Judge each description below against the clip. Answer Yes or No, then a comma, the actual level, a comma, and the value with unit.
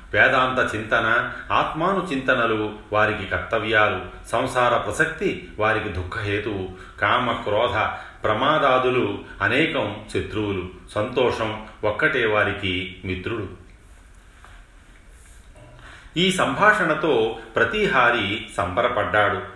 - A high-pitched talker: No, low, 105 Hz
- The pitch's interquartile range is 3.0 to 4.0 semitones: No, average, 4.4 semitones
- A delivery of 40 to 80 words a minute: Yes, slow, 70 wpm